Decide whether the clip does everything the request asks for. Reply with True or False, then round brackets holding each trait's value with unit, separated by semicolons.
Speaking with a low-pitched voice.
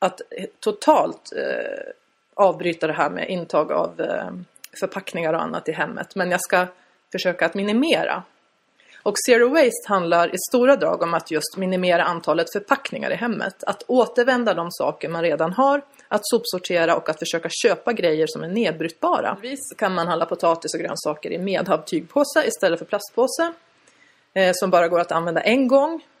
False (190 Hz)